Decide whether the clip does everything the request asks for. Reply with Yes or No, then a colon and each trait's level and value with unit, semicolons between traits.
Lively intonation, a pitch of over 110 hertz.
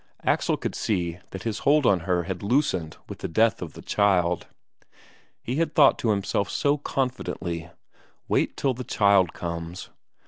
No: wide, 6.5 semitones; low, 100 Hz